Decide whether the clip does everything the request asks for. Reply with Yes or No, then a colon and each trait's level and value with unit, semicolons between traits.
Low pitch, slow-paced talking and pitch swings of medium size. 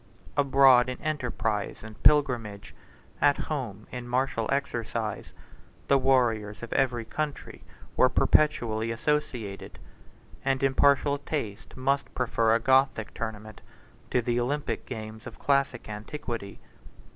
Yes: low, 125 Hz; slow, 115 wpm; average, 3.8 semitones